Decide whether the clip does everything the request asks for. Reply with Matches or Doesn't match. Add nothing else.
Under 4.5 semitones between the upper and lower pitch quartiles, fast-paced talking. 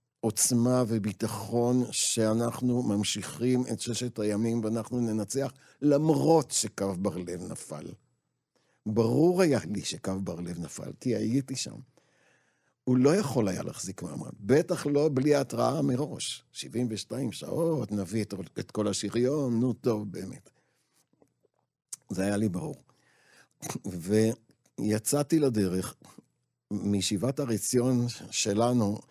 Doesn't match